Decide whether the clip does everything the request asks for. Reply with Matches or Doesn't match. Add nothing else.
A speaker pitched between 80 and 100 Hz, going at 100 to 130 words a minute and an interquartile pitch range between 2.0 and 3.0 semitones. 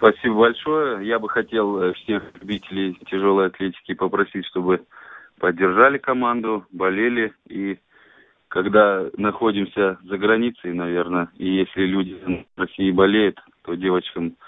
Matches